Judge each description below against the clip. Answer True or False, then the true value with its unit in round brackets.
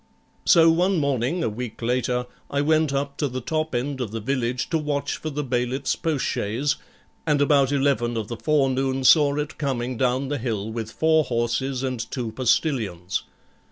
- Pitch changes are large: False (3.3 semitones)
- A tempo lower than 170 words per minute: False (175 wpm)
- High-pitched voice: False (135 Hz)